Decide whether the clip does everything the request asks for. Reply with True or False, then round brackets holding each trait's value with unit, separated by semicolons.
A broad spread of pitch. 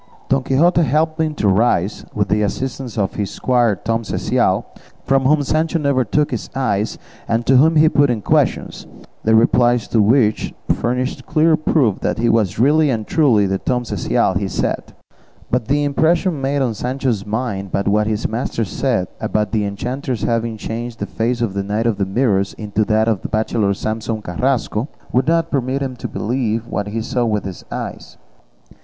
False (4.2 semitones)